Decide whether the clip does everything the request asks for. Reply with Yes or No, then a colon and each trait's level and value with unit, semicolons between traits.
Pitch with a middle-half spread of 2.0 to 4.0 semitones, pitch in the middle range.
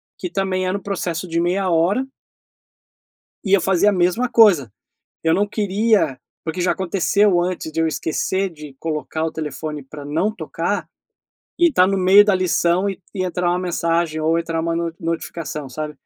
Yes: average, 3.0 semitones; medium, 175 Hz